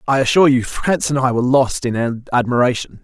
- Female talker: No, male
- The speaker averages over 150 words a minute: Yes, average, 200 wpm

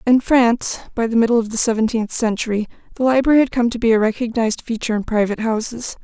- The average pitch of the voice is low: No, high, 230 Hz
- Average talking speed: No, fast, 210 wpm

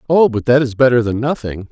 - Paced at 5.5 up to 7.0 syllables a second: Yes, 5.9 syllables/s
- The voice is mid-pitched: No, low, 125 Hz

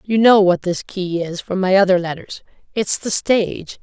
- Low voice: No, high, 190 Hz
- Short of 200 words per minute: No, fast, 205 wpm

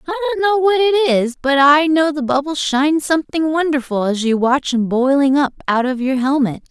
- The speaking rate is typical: No, fast, 215 wpm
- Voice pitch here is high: Yes, very high, 290 Hz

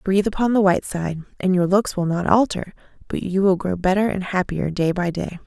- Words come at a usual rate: No, fast, 230 wpm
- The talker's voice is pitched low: No, medium, 185 Hz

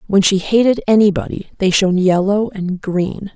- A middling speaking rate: Yes, average, 160 wpm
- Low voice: No, high, 195 Hz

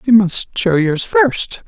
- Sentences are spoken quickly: No, average, 180 wpm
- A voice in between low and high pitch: Yes, medium, 175 Hz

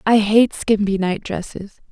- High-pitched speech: Yes, high, 205 Hz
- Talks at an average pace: Yes, average, 155 wpm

